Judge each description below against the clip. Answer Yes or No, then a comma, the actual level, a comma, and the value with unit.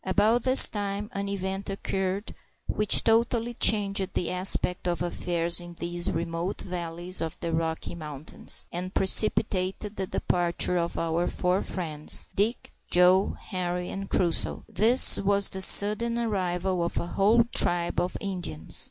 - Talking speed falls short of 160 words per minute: Yes, average, 145 wpm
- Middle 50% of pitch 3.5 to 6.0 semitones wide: No, average, 2.7 semitones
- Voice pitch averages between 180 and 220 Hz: Yes, medium, 185 Hz